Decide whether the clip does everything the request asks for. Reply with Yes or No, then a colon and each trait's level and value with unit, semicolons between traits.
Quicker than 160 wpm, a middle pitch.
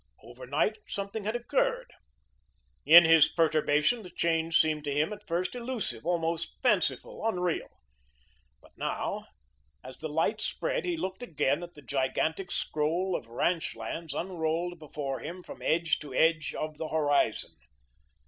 No: average, 145 wpm; medium, 165 Hz